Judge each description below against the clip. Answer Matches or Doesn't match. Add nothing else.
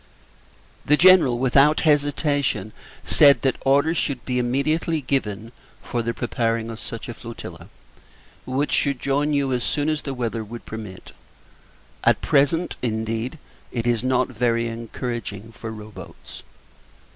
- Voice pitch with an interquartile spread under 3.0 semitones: Doesn't match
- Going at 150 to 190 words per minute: Doesn't match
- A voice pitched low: Matches